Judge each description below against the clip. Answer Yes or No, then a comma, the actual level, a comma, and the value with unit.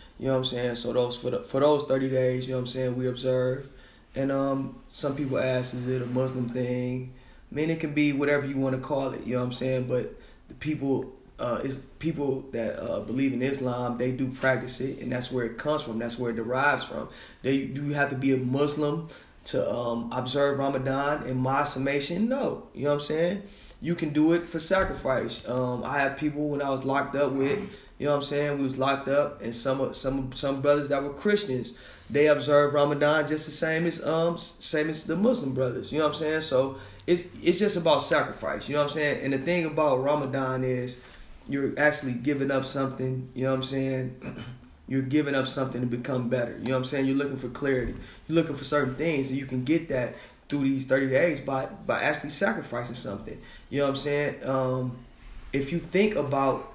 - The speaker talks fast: Yes, fast, 230 wpm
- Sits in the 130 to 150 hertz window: Yes, low, 135 Hz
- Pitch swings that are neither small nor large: No, narrow, 2.3 semitones